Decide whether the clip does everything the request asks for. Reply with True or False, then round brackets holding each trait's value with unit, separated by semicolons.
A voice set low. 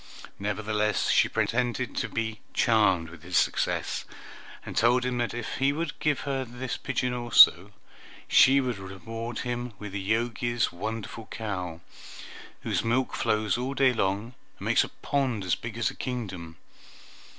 True (115 Hz)